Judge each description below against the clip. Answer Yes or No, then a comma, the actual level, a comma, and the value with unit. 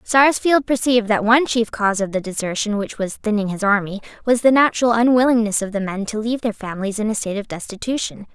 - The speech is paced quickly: Yes, fast, 215 wpm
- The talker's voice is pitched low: No, high, 220 Hz